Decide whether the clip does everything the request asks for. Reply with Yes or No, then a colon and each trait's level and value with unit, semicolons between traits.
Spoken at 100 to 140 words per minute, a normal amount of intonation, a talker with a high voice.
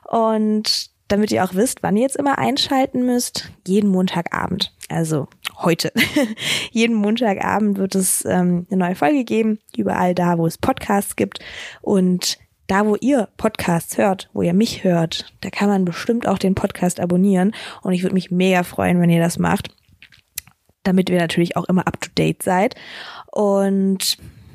No: average, 165 wpm; average, 3.2 semitones; high, 195 Hz